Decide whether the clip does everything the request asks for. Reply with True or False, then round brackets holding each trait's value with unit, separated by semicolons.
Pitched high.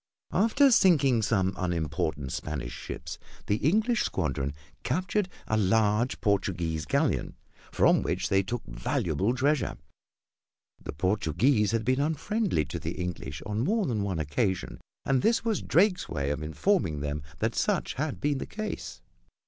False (105 Hz)